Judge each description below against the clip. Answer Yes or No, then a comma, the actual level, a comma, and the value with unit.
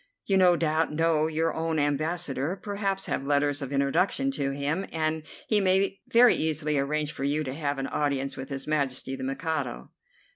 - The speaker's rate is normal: Yes, average, 180 wpm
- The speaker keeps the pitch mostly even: No, average, 3.1 semitones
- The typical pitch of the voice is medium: Yes, medium, 155 Hz